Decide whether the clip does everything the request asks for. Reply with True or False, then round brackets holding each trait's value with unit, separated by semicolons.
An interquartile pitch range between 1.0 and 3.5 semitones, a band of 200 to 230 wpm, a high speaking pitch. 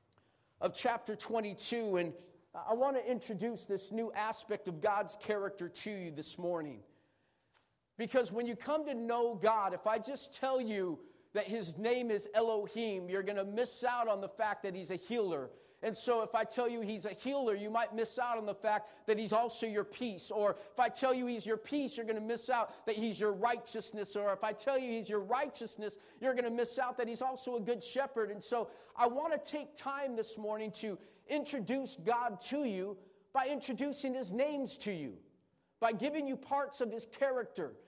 True (3.1 semitones; 205 wpm; 225 Hz)